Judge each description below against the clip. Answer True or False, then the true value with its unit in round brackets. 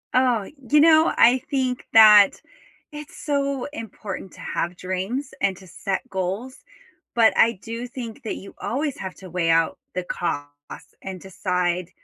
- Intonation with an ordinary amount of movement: False (5.7 semitones)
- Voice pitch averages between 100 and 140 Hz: False (215 Hz)